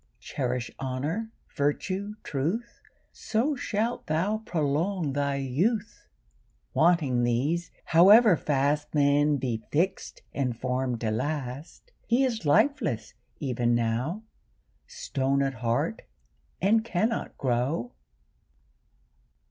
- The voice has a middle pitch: Yes, medium, 145 Hz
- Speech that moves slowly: Yes, slow, 100 wpm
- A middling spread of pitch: No, wide, 7.7 semitones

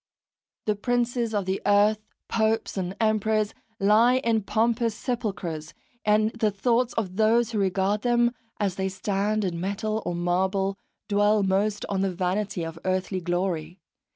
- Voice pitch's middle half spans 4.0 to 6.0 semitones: No, narrow, 2.6 semitones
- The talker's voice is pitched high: Yes, high, 205 Hz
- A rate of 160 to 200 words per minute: No, average, 150 wpm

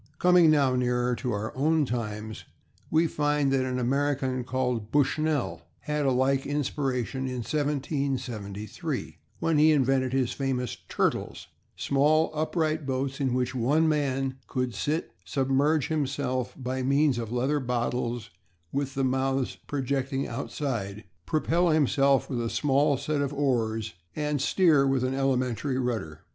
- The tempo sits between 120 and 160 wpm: Yes, average, 140 wpm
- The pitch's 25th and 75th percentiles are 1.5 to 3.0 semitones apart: Yes, narrow, 2.6 semitones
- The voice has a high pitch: No, low, 135 Hz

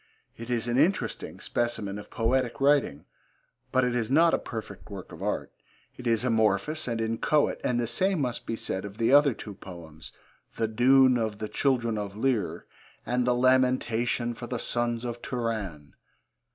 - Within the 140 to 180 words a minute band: Yes, average, 175 wpm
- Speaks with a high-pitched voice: No, low, 120 Hz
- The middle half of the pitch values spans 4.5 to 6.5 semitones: No, average, 2.7 semitones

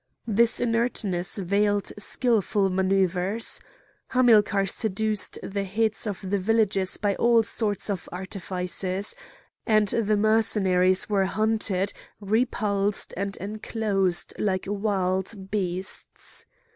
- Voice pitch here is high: Yes, high, 200 Hz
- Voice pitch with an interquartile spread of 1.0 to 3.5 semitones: Yes, narrow, 2.4 semitones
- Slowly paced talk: Yes, slow, 100 wpm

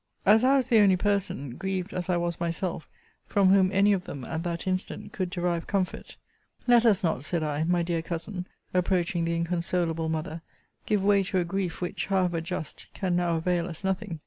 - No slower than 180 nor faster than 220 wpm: Yes, average, 200 wpm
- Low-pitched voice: No, medium, 180 Hz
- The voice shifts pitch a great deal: No, narrow, 2.4 semitones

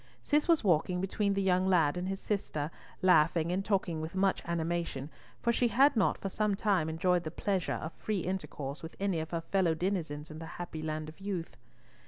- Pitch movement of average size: Yes, average, 3.5 semitones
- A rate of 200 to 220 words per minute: Yes, fast, 205 wpm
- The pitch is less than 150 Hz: No, medium, 180 Hz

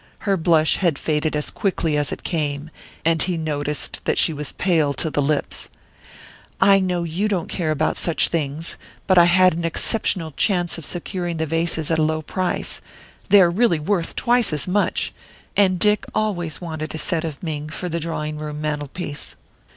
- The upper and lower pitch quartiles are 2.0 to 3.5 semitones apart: Yes, average, 3.0 semitones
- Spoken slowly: No, average, 185 wpm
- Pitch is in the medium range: Yes, medium, 165 Hz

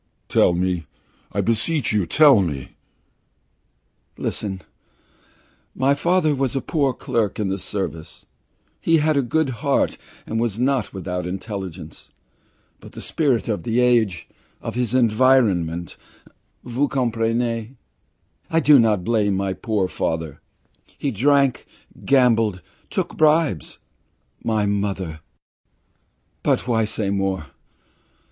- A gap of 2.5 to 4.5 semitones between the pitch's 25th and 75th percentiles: No, wide, 5.6 semitones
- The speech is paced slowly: Yes, slow, 120 wpm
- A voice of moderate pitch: No, low, 115 Hz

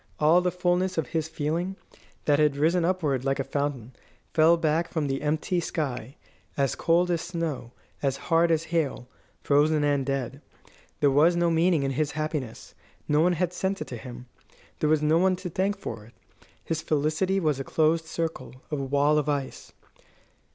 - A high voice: No, medium, 155 Hz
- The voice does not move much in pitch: No, average, 3.3 semitones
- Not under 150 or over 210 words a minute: Yes, average, 180 wpm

